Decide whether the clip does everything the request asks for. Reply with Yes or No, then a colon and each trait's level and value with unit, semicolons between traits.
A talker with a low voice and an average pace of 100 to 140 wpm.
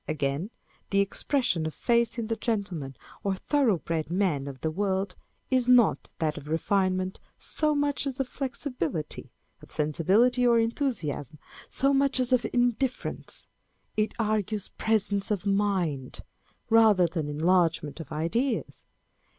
No: high, 200 Hz; slow, 135 wpm